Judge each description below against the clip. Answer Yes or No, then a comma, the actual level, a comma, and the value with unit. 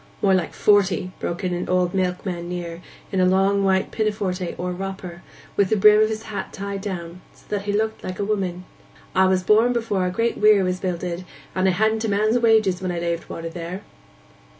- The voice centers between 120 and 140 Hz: No, high, 190 Hz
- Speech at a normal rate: No, fast, 210 wpm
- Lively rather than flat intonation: No, narrow, 2.6 semitones